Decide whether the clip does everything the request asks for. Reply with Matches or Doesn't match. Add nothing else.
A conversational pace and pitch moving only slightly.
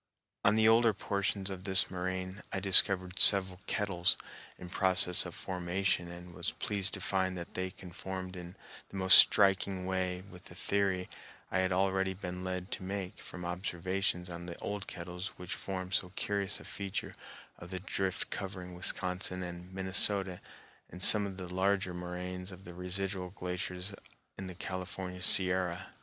Matches